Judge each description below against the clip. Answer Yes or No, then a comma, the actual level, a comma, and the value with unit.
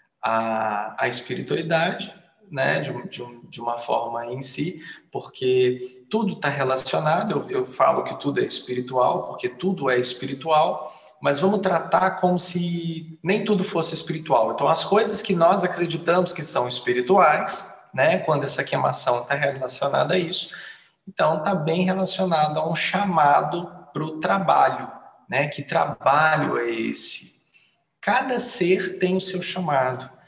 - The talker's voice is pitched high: No, medium, 165 Hz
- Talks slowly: No, average, 145 wpm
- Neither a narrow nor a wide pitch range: No, wide, 6.2 semitones